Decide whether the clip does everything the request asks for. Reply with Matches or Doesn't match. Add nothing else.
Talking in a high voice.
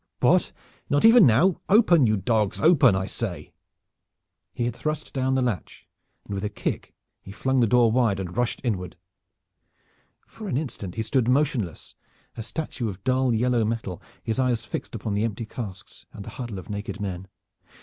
Doesn't match